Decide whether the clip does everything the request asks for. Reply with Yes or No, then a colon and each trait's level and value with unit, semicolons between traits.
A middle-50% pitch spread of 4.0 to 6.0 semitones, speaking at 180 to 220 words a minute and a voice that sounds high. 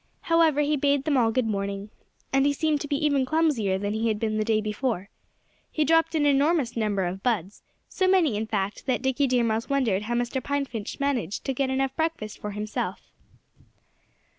Yes: average, 5.0 semitones; average, 200 wpm; very high, 255 Hz